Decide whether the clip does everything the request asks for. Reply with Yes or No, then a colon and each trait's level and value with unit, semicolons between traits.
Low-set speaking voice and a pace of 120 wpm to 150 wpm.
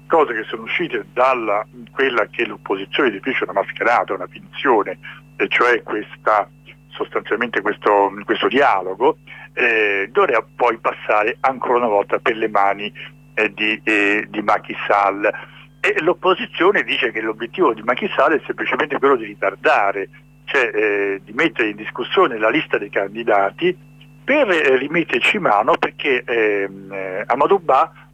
Yes: low, 110 Hz; average, 135 wpm